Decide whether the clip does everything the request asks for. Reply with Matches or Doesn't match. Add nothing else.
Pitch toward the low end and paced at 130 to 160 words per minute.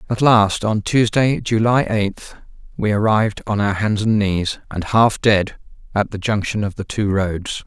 Doesn't match